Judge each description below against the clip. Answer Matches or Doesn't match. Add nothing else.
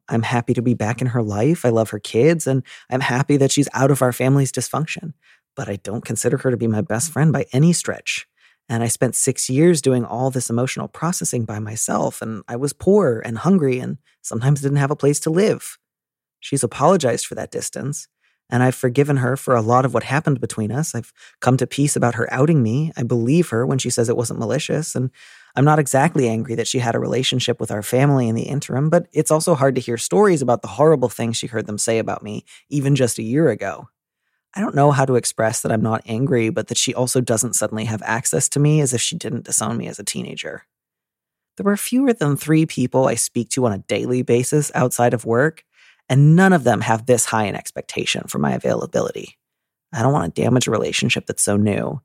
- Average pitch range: Matches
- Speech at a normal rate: Doesn't match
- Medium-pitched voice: Doesn't match